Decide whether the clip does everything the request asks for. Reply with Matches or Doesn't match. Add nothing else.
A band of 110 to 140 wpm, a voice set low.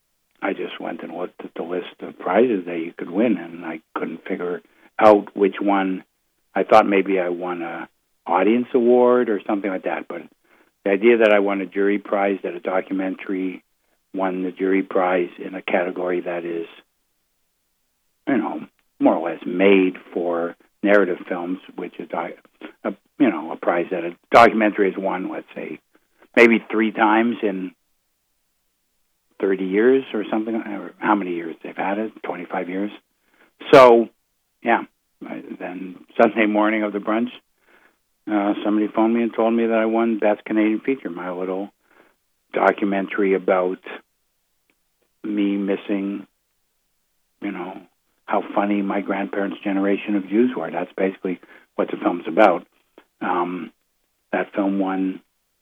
Doesn't match